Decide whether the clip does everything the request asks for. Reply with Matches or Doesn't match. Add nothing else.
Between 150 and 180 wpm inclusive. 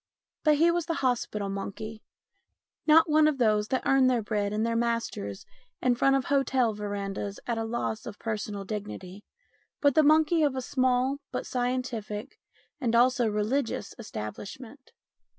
Matches